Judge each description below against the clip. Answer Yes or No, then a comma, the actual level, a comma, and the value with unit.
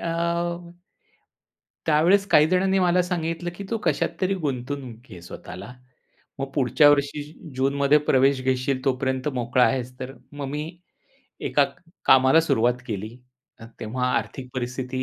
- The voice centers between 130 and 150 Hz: Yes, low, 135 Hz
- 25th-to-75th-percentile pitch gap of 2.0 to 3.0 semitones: No, average, 3.4 semitones